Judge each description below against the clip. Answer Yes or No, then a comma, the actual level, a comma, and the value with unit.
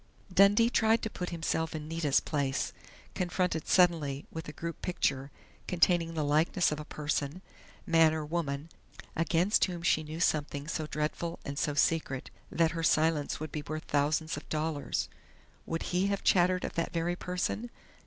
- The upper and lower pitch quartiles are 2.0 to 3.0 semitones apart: Yes, average, 2.7 semitones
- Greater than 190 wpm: No, average, 165 wpm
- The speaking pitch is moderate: Yes, medium, 160 Hz